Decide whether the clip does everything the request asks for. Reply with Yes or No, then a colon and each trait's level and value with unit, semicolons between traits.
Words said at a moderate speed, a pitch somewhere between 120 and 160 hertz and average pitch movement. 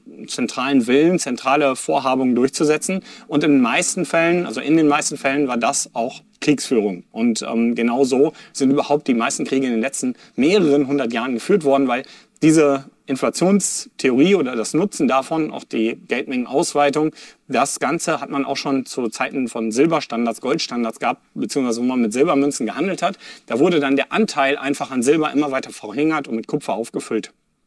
Yes: average, 175 wpm; medium, 140 Hz; average, 3.0 semitones